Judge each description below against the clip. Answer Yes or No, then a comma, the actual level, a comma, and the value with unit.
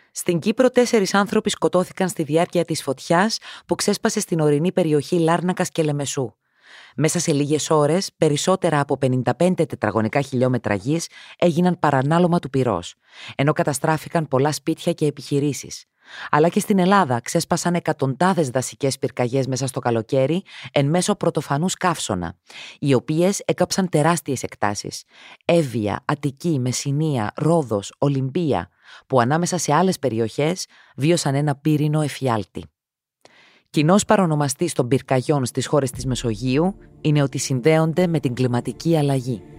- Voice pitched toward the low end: No, medium, 150 Hz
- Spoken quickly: No, average, 130 wpm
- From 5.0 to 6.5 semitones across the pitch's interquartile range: No, average, 4.6 semitones